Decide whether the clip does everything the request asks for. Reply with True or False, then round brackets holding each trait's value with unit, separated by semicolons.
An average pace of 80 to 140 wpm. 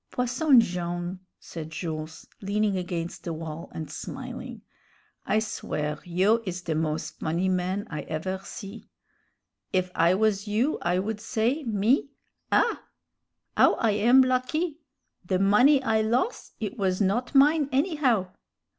True (135 wpm)